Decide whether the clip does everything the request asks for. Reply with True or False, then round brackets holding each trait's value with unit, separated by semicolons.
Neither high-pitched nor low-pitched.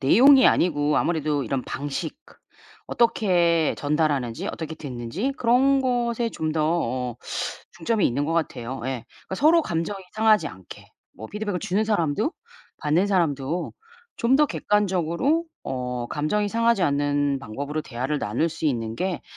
True (160 Hz)